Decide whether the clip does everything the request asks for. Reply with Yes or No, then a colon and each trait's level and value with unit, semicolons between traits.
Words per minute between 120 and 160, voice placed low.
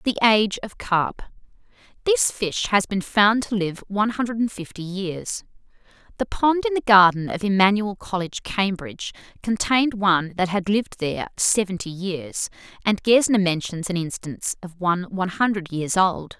No: average, 155 wpm; high, 195 Hz